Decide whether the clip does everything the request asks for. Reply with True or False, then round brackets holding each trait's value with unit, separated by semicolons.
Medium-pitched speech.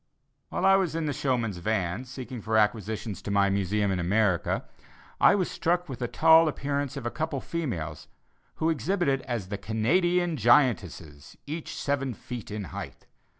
False (120 Hz)